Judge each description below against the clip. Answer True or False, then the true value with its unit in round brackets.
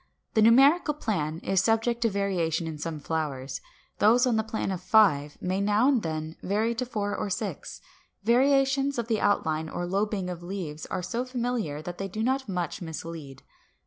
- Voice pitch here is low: False (200 Hz)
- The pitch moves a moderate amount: False (6.1 semitones)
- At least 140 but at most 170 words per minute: False (185 wpm)